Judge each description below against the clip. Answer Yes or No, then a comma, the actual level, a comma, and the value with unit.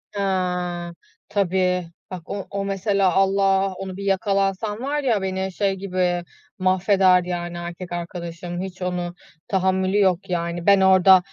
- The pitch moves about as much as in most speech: No, narrow, 1.7 semitones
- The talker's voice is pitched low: No, high, 190 Hz